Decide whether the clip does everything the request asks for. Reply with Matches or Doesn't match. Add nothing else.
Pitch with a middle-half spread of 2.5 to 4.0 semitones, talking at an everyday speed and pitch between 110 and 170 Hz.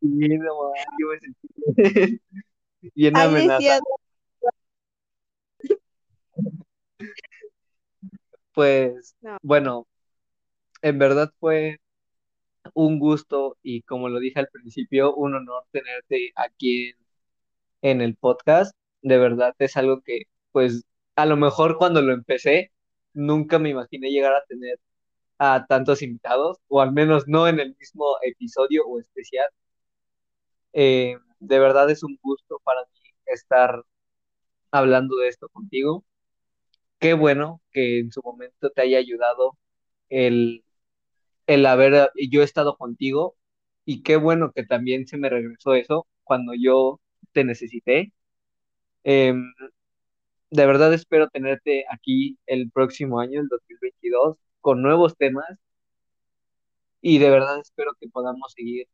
Doesn't match